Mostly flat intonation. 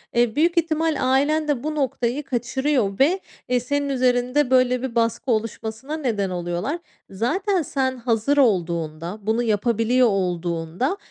No: average, 4.8 semitones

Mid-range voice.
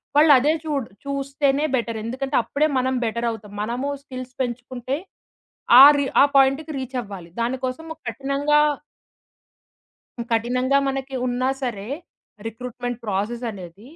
No: very high, 255 Hz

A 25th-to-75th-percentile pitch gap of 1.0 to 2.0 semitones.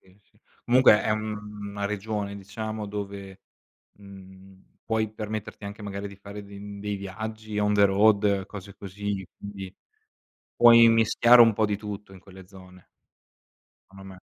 Yes: narrow, 1.6 semitones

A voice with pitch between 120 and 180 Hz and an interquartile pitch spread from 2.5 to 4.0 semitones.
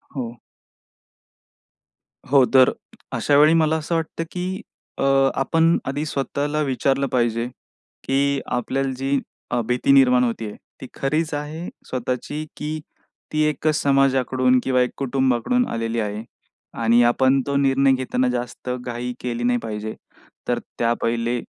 Yes: low, 135 Hz; average, 2.8 semitones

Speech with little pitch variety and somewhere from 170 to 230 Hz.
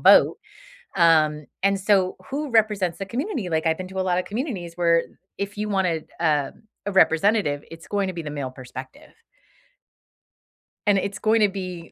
No: average, 3.8 semitones; medium, 185 Hz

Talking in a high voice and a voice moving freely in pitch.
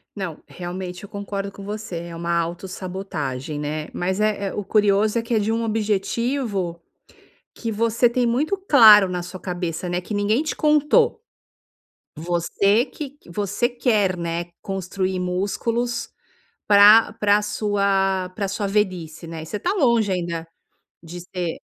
No: high, 200 Hz; average, 3.7 semitones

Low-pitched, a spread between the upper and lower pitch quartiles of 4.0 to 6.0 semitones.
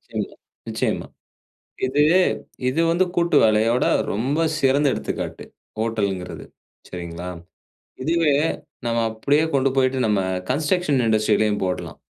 Yes: low, 120 Hz; wide, 5.5 semitones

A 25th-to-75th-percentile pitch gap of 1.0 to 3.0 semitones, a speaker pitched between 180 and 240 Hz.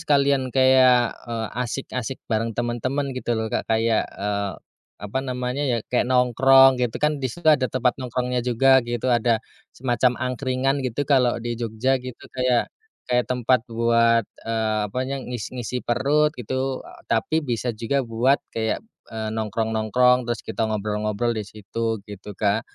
No: narrow, 2.6 semitones; low, 125 Hz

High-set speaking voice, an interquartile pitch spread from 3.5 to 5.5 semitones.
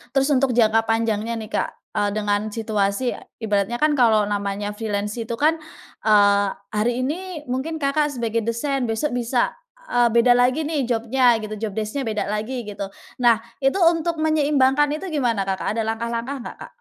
Yes: high, 235 Hz; average, 4.2 semitones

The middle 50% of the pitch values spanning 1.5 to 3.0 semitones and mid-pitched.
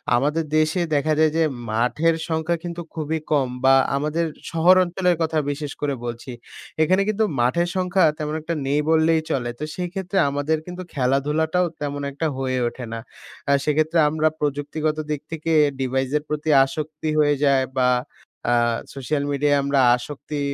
Yes: average, 2.7 semitones; medium, 150 Hz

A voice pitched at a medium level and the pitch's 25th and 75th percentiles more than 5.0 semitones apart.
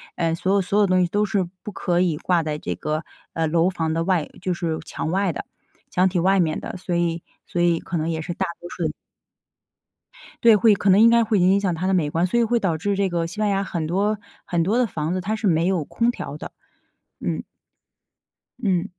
No: medium, 180 Hz; average, 3.2 semitones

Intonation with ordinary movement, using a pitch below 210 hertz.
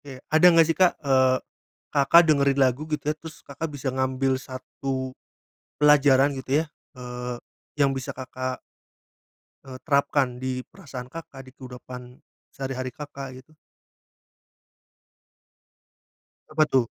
No: narrow, 2.1 semitones; low, 135 Hz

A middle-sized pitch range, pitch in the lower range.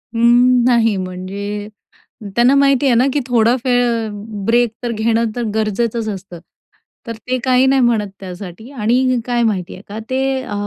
No: average, 3.3 semitones; high, 235 Hz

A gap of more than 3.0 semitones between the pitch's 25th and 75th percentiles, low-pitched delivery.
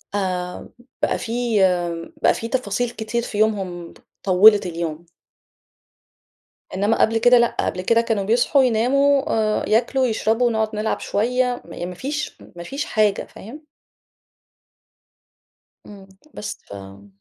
No: average, 4.3 semitones; high, 220 Hz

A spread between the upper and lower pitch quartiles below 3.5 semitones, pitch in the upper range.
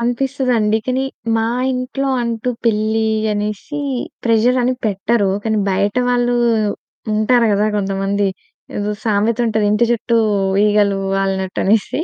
Yes: average, 2.9 semitones; high, 220 Hz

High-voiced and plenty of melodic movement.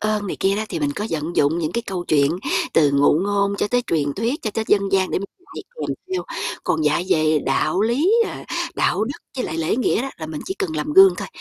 Yes: high, 195 Hz; wide, 6.6 semitones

